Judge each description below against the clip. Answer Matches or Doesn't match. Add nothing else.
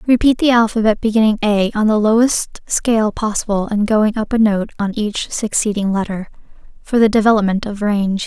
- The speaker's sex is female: Matches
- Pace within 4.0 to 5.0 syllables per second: Doesn't match